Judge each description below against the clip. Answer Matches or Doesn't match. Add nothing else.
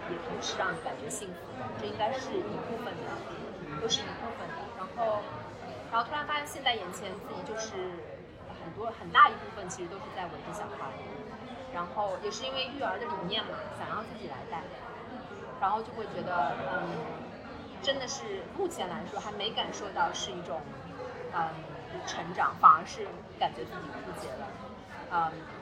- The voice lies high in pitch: Matches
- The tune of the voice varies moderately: Matches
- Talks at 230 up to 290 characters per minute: Matches